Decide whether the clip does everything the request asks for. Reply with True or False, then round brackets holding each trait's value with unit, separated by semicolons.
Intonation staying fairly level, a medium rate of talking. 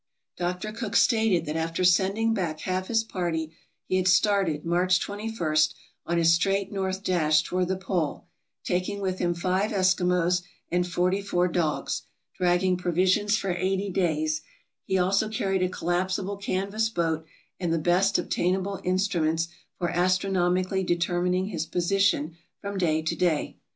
True (2.0 semitones; 145 wpm)